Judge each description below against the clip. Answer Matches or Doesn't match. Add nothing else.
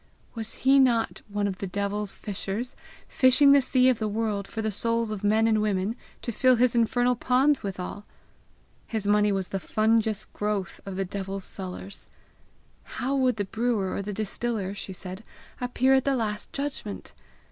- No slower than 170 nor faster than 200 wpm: Matches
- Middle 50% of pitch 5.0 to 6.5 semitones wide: Doesn't match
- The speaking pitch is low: Doesn't match